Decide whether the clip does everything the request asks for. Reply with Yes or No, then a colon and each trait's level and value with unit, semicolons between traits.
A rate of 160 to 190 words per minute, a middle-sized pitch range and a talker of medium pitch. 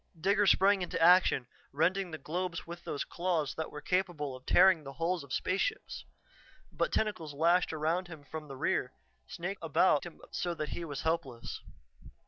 Yes: average, 170 wpm; average, 3.4 semitones; medium, 165 Hz